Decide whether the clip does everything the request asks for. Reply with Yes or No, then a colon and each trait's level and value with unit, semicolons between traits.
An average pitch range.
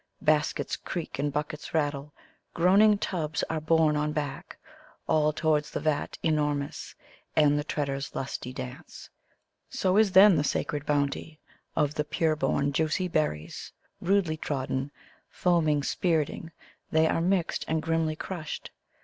No: narrow, 2.0 semitones